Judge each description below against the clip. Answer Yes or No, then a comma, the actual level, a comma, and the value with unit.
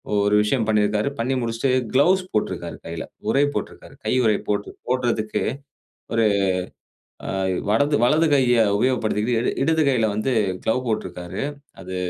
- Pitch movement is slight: No, average, 3.8 semitones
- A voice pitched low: Yes, low, 115 Hz